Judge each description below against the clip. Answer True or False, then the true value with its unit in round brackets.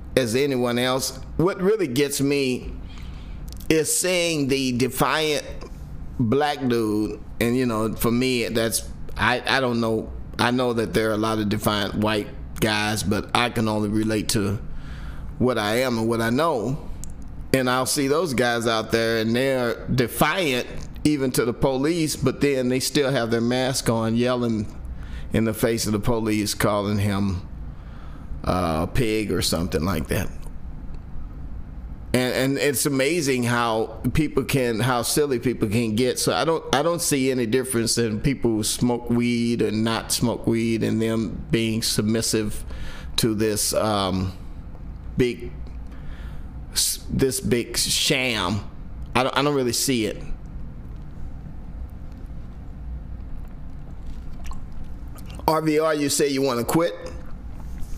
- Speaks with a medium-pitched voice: False (115 Hz)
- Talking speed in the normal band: True (145 wpm)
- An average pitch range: False (6.5 semitones)